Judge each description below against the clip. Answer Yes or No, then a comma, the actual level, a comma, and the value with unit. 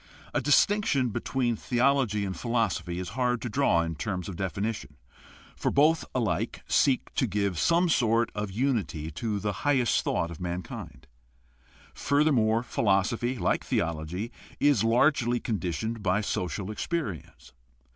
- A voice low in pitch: Yes, low, 110 Hz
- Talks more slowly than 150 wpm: Yes, average, 140 wpm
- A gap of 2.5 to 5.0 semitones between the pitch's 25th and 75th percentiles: No, wide, 5.6 semitones